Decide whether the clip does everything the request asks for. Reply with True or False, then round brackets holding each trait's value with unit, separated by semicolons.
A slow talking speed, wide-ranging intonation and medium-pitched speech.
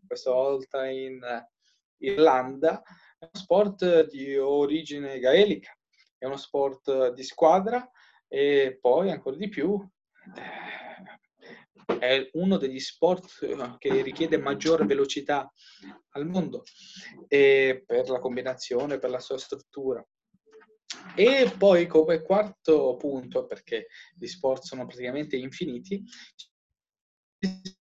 True (100 wpm; 6.9 semitones; 160 Hz)